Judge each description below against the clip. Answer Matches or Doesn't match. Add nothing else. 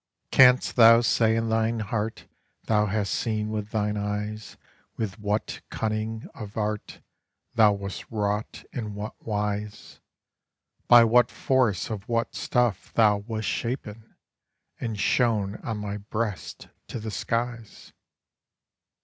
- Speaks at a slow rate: Matches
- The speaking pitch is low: Matches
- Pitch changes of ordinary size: Doesn't match